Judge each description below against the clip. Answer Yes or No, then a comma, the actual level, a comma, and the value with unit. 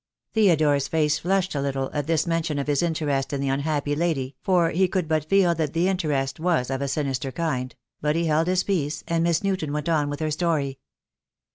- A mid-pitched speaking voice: Yes, medium, 155 Hz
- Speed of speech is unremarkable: No, fast, 215 wpm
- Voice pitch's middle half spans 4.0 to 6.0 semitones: No, average, 3.2 semitones